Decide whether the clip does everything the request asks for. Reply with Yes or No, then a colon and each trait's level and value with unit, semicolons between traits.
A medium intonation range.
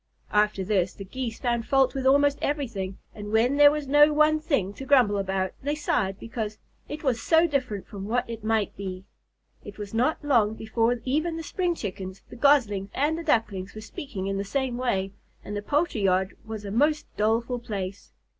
No: wide, 5.9 semitones